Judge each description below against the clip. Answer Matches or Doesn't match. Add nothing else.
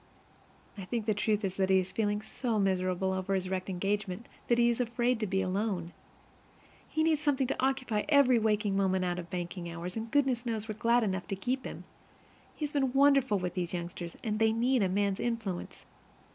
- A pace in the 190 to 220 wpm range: Matches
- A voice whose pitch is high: Matches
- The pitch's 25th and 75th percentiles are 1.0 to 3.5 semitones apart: Doesn't match